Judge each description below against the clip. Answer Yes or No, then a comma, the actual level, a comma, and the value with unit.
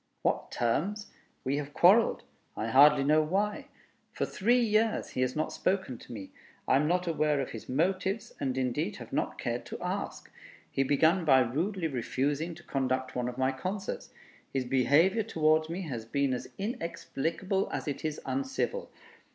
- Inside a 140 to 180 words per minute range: Yes, average, 170 wpm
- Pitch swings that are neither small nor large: No, wide, 6.3 semitones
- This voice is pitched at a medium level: Yes, medium, 155 Hz